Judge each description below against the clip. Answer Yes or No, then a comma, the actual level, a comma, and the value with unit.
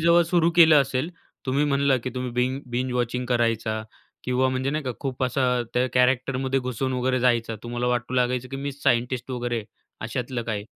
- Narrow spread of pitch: Yes, narrow, 1.8 semitones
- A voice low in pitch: Yes, low, 125 Hz